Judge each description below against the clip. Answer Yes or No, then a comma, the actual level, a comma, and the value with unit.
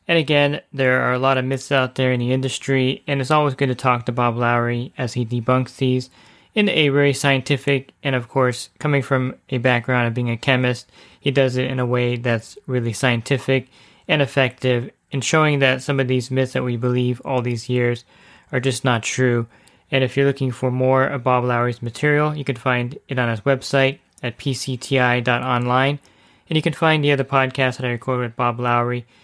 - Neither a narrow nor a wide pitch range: No, narrow, 1.9 semitones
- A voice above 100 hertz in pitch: Yes, low, 130 Hz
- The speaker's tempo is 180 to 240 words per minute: Yes, fast, 205 wpm